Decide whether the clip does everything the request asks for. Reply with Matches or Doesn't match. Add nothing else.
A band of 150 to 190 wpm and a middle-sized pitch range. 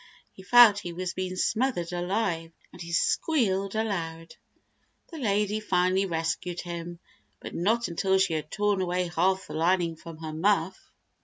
Matches